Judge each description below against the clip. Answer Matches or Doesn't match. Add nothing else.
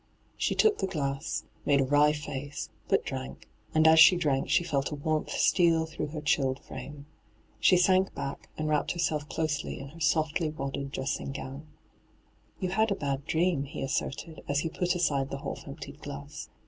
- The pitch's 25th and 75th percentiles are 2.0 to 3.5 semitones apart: Matches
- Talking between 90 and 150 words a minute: Doesn't match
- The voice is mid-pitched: Matches